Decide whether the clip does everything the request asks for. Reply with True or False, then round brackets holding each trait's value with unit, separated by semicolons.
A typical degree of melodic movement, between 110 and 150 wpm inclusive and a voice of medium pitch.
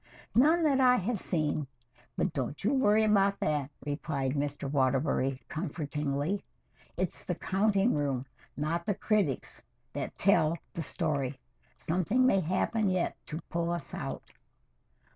False (5.9 semitones; 135 wpm; 165 Hz)